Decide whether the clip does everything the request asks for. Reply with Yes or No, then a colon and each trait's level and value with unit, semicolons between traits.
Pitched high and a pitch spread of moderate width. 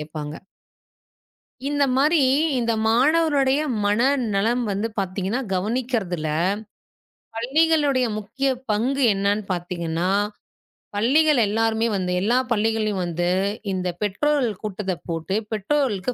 No: high, 220 Hz; wide, 5.8 semitones